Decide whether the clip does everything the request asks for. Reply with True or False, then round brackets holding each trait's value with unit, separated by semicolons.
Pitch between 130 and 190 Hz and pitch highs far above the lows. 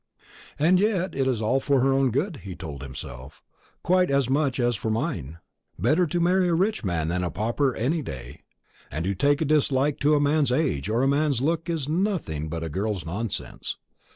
True (135 Hz; 7.9 semitones)